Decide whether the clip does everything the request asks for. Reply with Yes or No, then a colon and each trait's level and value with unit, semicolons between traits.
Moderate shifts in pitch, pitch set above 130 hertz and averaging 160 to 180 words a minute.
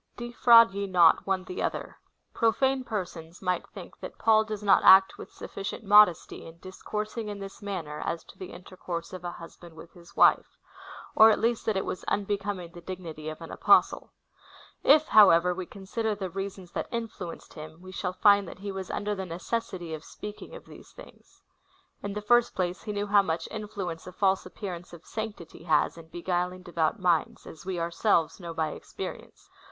No: average, 3.3 semitones; high, 190 Hz; average, 195 wpm